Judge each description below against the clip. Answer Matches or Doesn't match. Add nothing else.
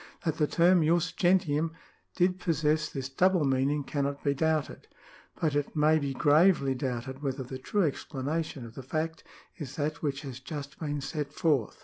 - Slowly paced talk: Doesn't match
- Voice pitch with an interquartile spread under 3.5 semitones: Matches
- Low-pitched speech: Doesn't match